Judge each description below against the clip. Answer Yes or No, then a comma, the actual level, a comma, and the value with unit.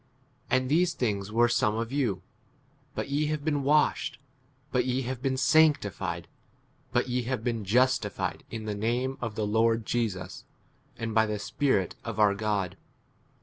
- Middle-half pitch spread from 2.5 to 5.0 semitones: Yes, average, 3.7 semitones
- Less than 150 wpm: No, average, 160 wpm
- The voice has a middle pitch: No, low, 115 Hz